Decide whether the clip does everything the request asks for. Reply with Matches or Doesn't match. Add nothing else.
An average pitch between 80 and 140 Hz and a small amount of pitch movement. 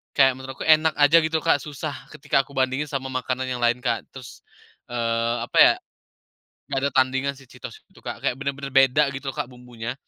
Matches